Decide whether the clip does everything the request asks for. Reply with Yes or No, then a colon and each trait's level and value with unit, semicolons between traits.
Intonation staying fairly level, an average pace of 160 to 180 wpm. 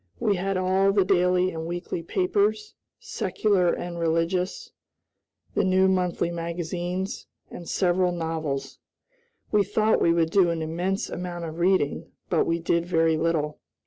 No: narrow, 2.1 semitones; average, 145 wpm